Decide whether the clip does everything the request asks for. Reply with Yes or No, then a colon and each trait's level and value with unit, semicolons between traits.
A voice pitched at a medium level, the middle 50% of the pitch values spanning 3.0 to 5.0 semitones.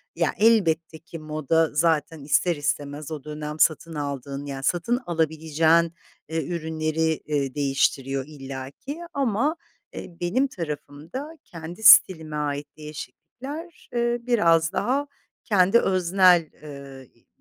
Yes: medium, 160 Hz; average, 3.9 semitones